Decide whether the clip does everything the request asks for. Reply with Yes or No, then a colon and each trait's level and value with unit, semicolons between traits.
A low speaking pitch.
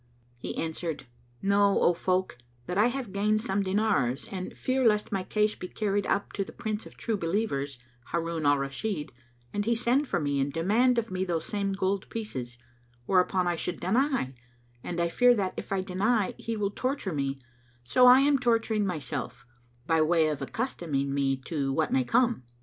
No: high, 190 Hz